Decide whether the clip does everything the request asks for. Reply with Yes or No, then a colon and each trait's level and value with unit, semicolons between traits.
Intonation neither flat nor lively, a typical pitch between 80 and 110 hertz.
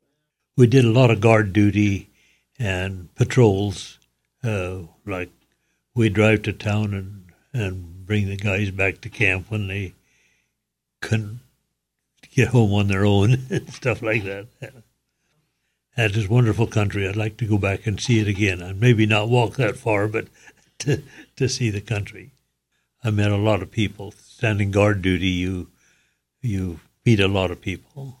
Yes: average, 3.3 semitones; low, 105 Hz